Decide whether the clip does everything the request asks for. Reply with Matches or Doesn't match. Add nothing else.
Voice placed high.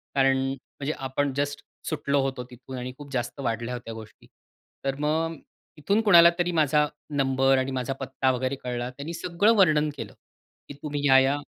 Doesn't match